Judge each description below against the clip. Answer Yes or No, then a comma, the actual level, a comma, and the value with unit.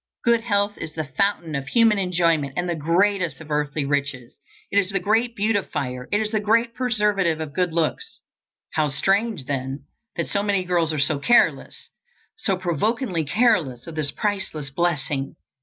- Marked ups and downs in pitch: Yes, wide, 5.8 semitones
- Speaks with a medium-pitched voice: Yes, medium, 175 Hz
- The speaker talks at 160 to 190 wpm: Yes, average, 170 wpm